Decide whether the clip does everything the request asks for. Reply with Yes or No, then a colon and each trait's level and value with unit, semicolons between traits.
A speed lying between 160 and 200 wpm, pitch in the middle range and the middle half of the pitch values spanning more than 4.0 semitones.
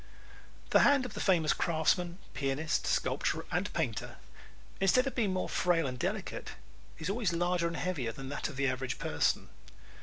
Yes: average, 170 wpm; medium, 170 Hz; average, 5.1 semitones